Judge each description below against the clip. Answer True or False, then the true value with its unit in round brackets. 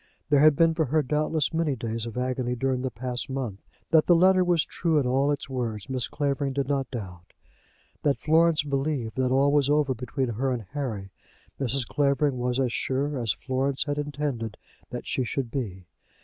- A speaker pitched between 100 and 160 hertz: True (135 Hz)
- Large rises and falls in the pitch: False (3.0 semitones)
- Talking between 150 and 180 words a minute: False (190 wpm)